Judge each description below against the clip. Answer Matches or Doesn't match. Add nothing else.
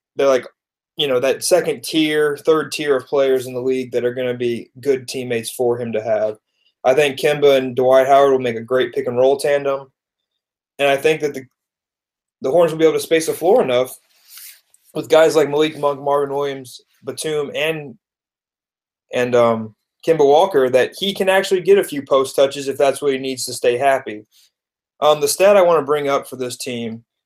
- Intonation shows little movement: Doesn't match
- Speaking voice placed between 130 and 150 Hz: Matches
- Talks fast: Matches